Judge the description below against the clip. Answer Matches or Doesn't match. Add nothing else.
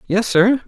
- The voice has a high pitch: Matches